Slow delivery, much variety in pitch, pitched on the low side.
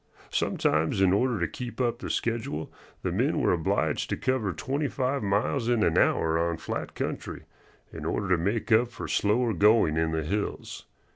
No: average, 185 wpm; wide, 6.2 semitones; low, 105 Hz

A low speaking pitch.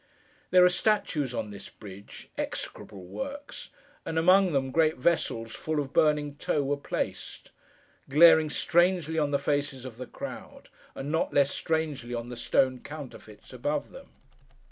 No: medium, 145 Hz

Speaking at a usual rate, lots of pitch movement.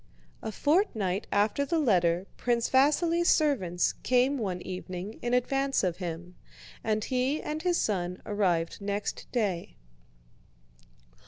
No: slow, 120 wpm; wide, 6.9 semitones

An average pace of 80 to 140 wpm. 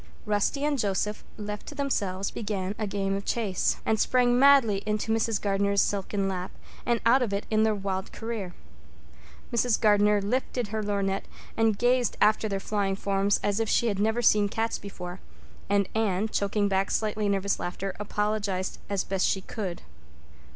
No: average, 170 wpm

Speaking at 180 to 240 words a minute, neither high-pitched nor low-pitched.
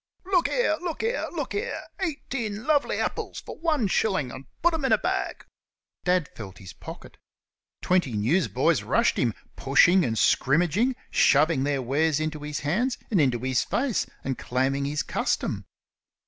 No: average, 160 wpm; medium, 160 Hz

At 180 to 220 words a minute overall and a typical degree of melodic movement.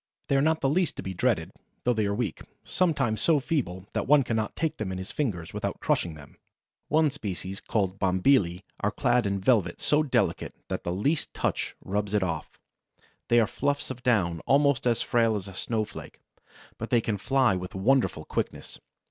No: average, 190 wpm; wide, 6.3 semitones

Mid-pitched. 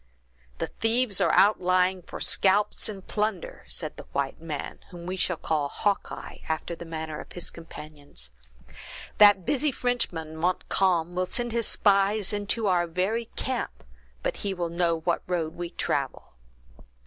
Yes: medium, 180 Hz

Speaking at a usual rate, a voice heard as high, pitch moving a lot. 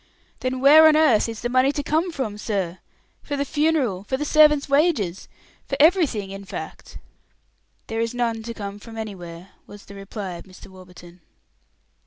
Yes: average, 175 wpm; high, 230 Hz; wide, 6.6 semitones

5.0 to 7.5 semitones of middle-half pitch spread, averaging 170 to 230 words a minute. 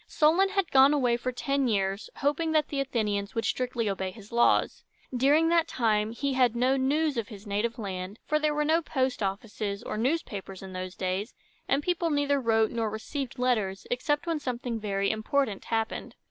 Yes: average, 5.3 semitones; average, 190 wpm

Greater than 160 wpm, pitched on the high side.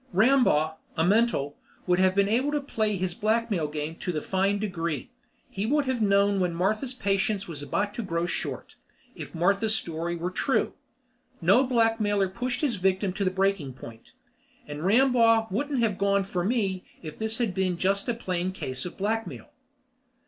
Yes: average, 175 wpm; high, 200 Hz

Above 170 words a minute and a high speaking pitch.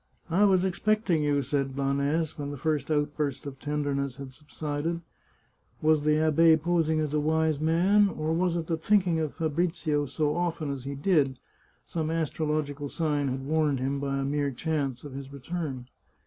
No: average, 180 wpm; medium, 150 Hz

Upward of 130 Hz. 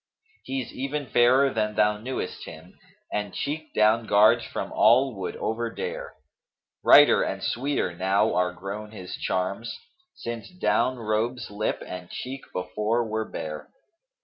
No: low, 110 Hz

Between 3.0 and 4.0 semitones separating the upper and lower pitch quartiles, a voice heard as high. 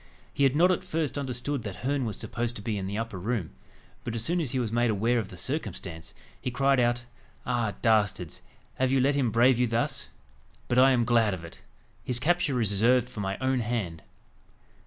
No: average, 3.6 semitones; low, 120 Hz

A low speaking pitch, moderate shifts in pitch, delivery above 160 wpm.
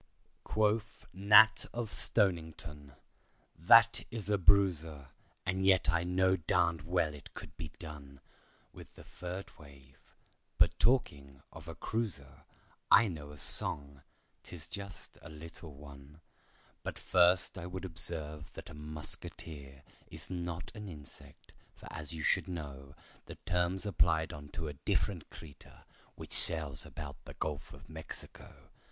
No: very low, 80 Hz; average, 4.1 semitones; slow, 135 wpm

